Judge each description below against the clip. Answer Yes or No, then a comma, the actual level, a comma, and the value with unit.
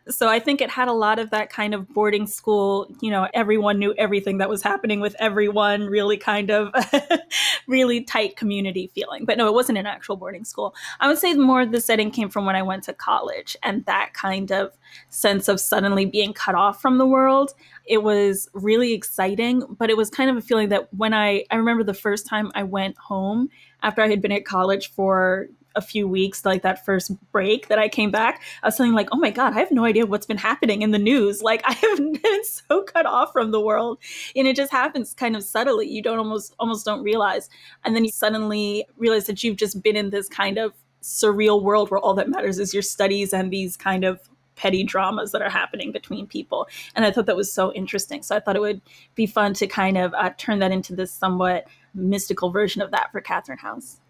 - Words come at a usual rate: No, fast, 230 wpm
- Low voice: No, high, 210 Hz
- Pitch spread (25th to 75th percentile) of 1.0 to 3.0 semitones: Yes, narrow, 2.6 semitones